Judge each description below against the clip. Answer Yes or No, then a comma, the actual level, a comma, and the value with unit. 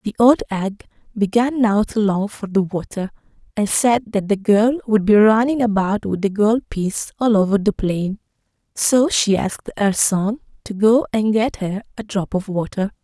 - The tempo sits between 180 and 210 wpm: Yes, average, 190 wpm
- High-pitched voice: Yes, high, 210 Hz